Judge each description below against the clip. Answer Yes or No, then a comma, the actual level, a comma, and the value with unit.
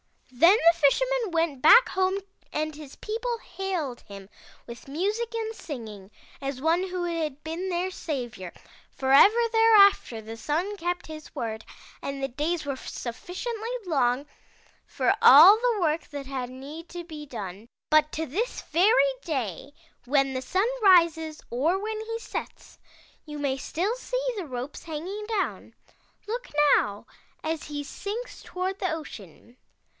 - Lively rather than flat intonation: Yes, wide, 6.6 semitones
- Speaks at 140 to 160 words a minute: Yes, average, 150 wpm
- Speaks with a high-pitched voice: Yes, very high, 320 Hz